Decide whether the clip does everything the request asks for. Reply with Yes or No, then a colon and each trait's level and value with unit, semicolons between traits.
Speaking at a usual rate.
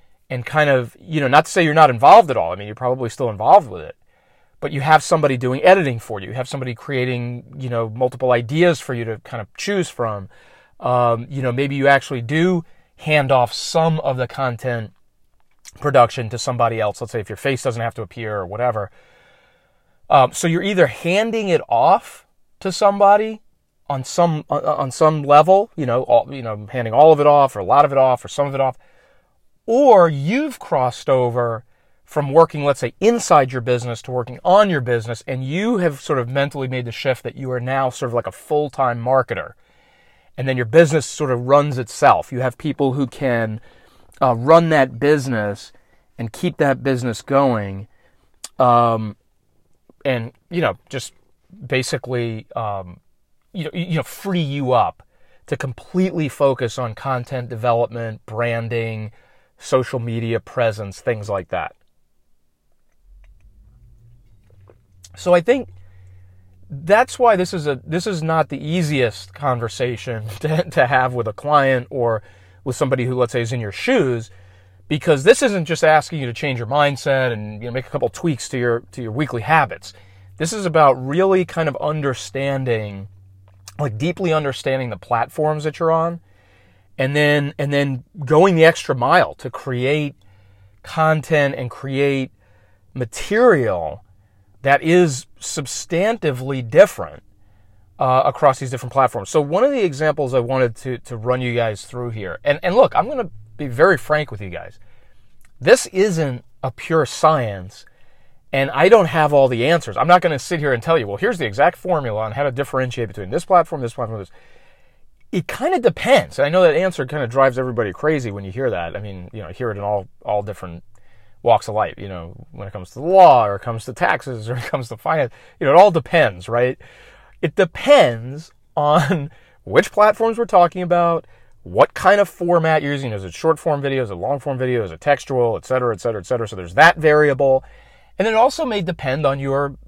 Yes: average, 190 wpm